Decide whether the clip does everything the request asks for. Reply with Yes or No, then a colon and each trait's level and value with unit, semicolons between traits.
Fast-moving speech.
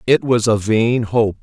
Yes: fast, 210 wpm